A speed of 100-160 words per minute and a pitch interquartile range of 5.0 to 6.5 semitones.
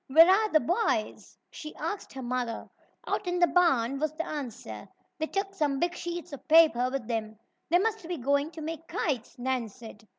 No: average, 195 wpm; wide, 5.6 semitones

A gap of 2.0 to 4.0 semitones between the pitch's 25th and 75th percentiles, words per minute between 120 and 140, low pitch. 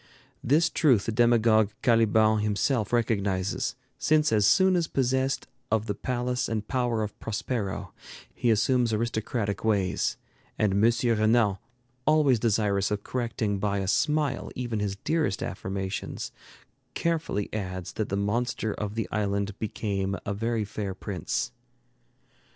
Yes: average, 3.3 semitones; slow, 135 wpm; low, 110 Hz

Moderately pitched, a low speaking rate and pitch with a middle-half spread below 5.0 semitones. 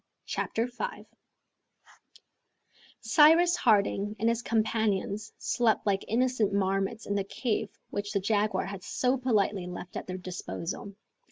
No: high, 210 Hz; slow, 125 wpm; average, 2.9 semitones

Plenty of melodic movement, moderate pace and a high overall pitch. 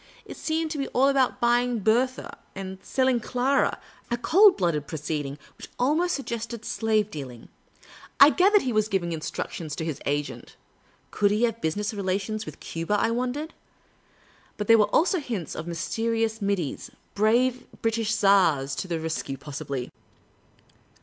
Yes: wide, 6.7 semitones; average, 165 wpm; high, 215 Hz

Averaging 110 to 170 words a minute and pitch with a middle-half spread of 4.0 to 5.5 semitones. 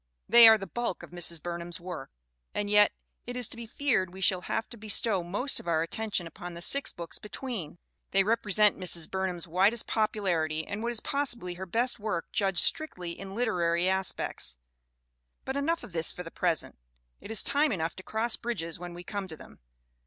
No: fast, 205 wpm; average, 4.7 semitones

